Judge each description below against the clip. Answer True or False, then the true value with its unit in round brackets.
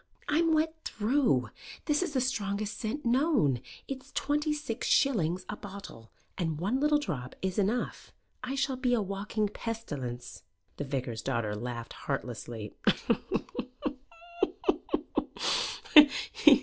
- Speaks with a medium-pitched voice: False (210 Hz)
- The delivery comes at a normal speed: False (115 wpm)